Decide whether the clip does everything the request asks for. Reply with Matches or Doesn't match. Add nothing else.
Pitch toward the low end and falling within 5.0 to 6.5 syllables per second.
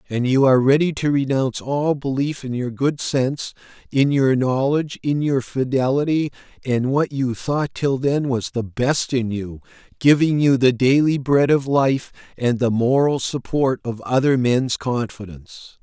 Doesn't match